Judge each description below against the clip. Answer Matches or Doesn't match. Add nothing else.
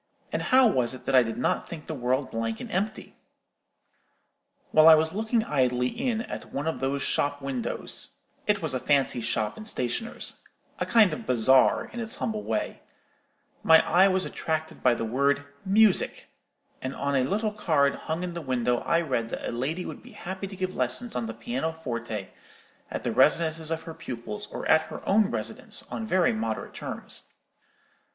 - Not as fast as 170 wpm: Doesn't match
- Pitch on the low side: Doesn't match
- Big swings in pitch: Matches